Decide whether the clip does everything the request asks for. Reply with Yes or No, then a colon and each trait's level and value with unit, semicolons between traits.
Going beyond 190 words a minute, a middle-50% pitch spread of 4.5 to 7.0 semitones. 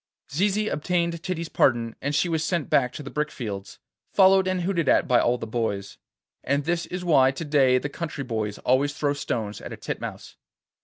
Yes: average, 200 wpm; wide, 5.5 semitones